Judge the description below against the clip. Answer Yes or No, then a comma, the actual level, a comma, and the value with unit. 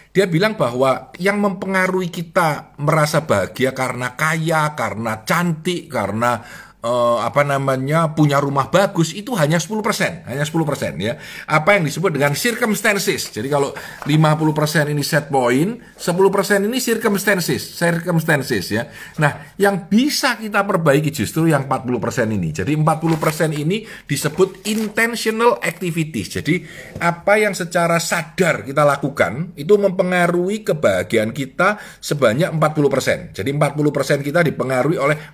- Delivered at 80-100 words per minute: No, average, 125 wpm